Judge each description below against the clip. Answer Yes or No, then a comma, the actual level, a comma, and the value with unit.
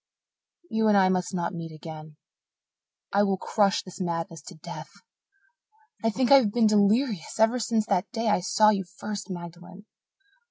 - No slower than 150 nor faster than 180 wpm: Yes, average, 165 wpm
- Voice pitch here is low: No, high, 195 Hz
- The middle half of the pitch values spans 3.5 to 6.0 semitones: Yes, average, 3.8 semitones